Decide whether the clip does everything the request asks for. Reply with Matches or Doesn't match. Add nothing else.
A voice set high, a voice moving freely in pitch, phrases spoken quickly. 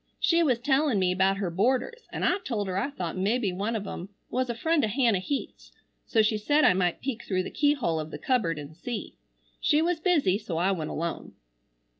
Matches